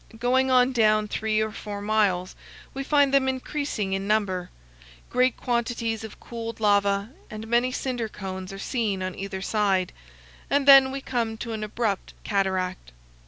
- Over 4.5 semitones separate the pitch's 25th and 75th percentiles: No, average, 3.9 semitones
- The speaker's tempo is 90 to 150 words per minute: No, average, 160 wpm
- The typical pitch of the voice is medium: No, high, 220 Hz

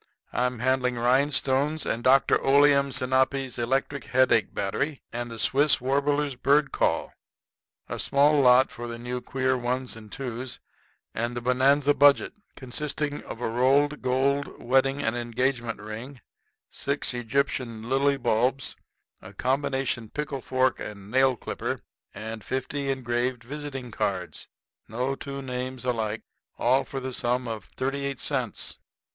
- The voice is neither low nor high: No, low, 130 Hz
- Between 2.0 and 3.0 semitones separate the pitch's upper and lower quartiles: Yes, narrow, 2.5 semitones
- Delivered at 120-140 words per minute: Yes, slow, 135 wpm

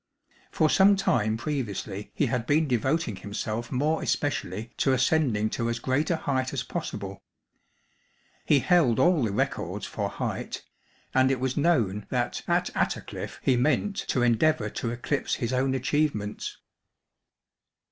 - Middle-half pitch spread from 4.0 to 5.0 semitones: Yes, average, 4.7 semitones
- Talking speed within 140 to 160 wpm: Yes, average, 145 wpm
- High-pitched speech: No, low, 130 Hz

